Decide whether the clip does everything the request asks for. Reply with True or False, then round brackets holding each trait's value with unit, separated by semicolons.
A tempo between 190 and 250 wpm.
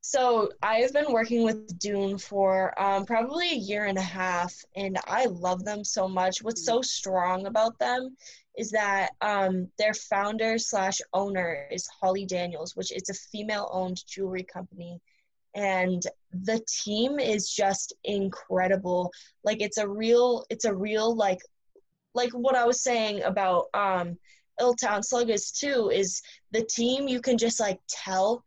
False (155 wpm)